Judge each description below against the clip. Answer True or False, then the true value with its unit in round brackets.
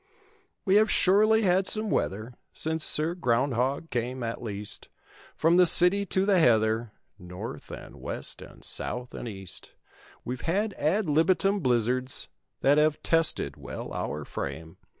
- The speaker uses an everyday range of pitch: False (7.8 semitones)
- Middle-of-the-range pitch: True (150 Hz)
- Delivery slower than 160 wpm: True (145 wpm)